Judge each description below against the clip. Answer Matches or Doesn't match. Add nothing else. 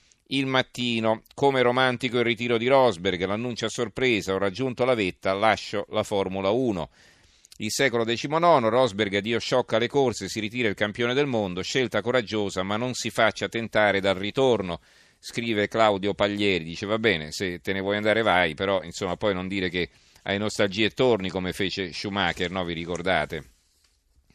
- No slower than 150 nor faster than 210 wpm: Matches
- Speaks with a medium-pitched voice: Doesn't match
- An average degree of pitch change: Matches